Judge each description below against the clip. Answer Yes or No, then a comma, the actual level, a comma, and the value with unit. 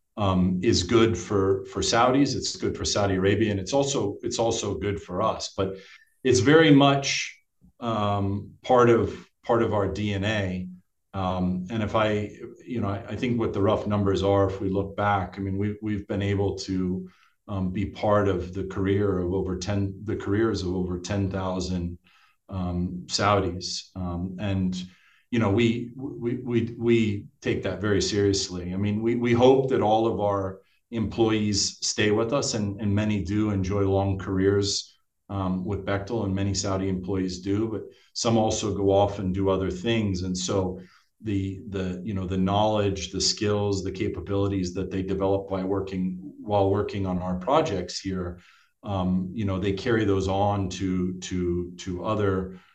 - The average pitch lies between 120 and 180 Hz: No, low, 100 Hz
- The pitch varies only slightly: Yes, narrow, 1.9 semitones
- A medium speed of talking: Yes, average, 175 wpm